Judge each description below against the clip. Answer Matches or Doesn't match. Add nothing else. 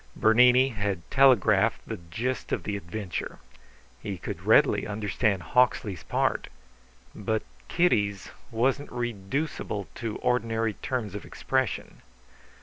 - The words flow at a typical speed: Doesn't match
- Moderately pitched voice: Doesn't match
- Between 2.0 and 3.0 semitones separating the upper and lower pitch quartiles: Doesn't match